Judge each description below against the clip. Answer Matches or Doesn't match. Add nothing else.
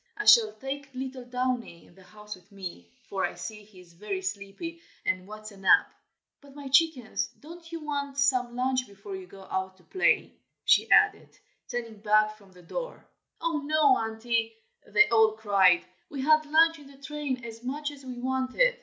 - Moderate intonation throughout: Doesn't match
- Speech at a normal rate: Matches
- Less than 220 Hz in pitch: Doesn't match